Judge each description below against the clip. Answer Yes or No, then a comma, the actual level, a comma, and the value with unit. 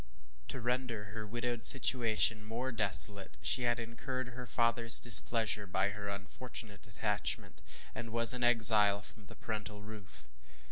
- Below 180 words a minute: Yes, average, 140 wpm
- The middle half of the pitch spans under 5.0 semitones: Yes, narrow, 2.5 semitones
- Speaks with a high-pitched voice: No, low, 115 Hz